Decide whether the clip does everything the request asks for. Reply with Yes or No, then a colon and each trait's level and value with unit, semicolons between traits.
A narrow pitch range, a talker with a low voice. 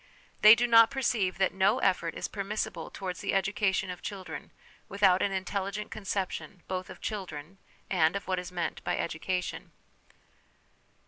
No: narrow, 1.8 semitones; high, 190 Hz